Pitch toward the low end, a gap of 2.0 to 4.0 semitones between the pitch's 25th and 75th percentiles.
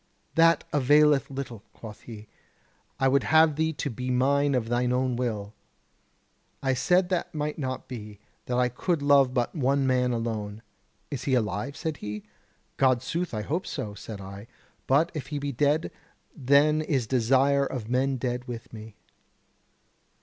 Yes: low, 130 Hz; average, 3.4 semitones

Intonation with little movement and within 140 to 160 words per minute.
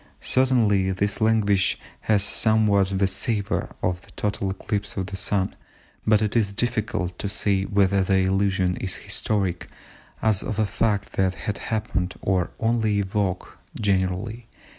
Yes: narrow, 2.1 semitones; average, 150 wpm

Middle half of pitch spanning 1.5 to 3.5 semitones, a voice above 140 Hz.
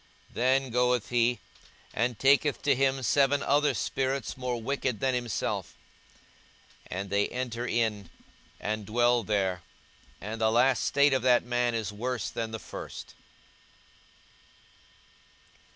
No: average, 3.0 semitones; low, 120 Hz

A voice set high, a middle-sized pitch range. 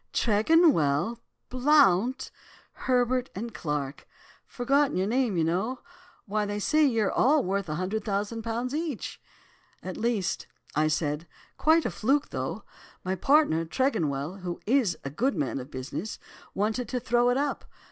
No: high, 220 Hz; wide, 6.6 semitones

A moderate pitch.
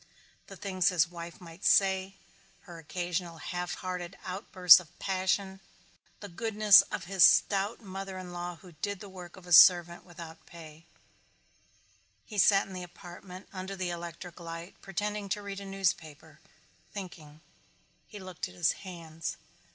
Yes: medium, 180 Hz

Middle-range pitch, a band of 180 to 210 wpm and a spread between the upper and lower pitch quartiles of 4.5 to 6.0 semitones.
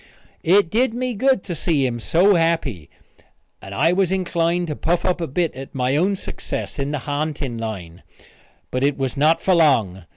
Yes: medium, 155 Hz; average, 190 wpm; average, 5.2 semitones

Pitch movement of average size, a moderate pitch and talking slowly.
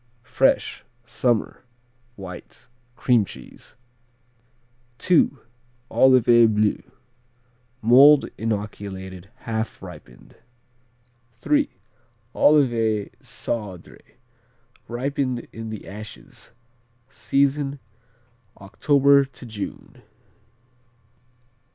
No: average, 4.5 semitones; low, 115 Hz; slow, 65 wpm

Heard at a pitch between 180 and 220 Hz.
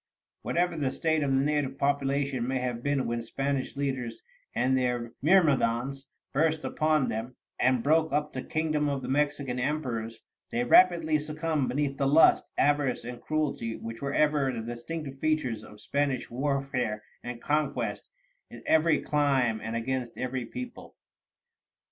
No: low, 135 Hz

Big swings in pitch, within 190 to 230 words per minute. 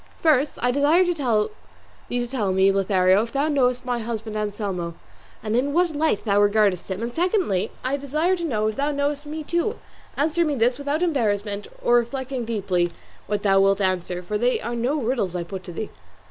Yes: wide, 6.2 semitones; average, 195 wpm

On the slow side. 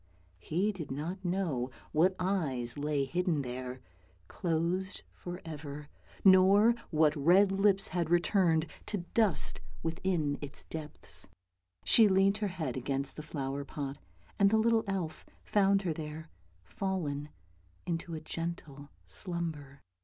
Yes: slow, 130 wpm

